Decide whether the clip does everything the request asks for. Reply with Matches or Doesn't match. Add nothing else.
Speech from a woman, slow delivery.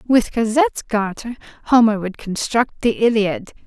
Matches